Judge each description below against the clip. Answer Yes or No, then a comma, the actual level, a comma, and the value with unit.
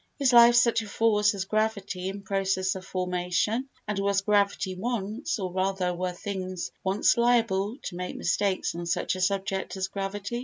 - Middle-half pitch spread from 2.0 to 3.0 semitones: Yes, narrow, 2.4 semitones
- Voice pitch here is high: Yes, high, 195 Hz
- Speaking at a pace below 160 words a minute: No, average, 165 wpm